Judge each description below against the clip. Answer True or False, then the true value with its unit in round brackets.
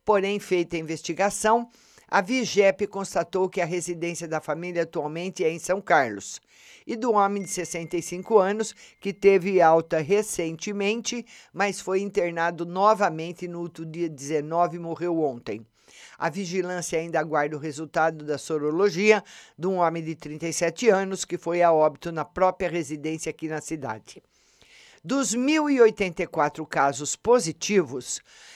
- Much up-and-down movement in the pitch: False (3.6 semitones)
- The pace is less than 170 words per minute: True (140 wpm)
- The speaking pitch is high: False (175 Hz)